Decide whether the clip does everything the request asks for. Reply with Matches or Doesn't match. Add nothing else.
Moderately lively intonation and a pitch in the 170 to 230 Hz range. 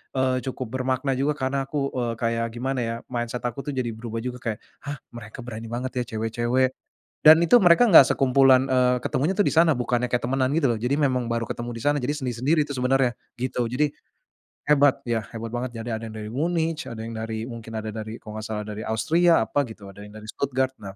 Doesn't match